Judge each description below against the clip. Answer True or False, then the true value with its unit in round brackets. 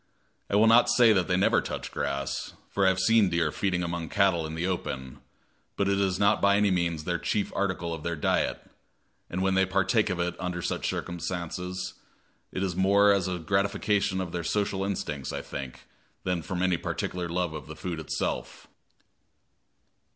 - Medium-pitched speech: False (90 Hz)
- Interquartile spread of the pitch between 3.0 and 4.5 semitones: False (2.4 semitones)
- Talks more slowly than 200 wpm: True (190 wpm)